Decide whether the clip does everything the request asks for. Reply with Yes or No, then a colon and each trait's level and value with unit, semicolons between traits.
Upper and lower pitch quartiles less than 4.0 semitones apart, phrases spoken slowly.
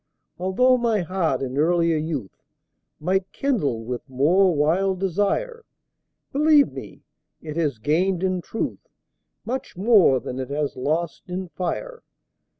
No: average, 4.9 semitones; slow, 130 wpm